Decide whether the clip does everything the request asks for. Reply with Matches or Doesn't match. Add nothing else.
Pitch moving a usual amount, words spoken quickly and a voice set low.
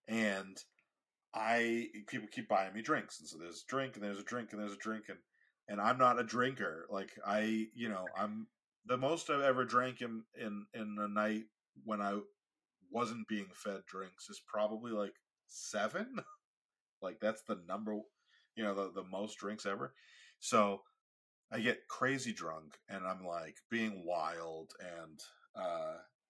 Doesn't match